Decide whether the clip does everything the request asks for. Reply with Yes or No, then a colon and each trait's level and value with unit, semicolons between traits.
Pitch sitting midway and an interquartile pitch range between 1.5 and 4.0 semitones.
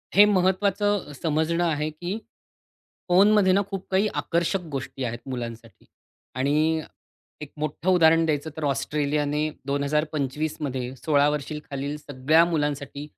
Yes: medium, 150 Hz; average, 3.5 semitones